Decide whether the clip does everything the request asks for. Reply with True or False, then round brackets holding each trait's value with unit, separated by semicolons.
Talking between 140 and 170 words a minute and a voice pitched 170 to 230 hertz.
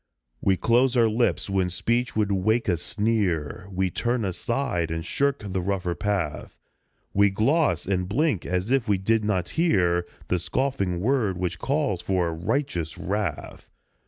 False (155 wpm; 100 Hz)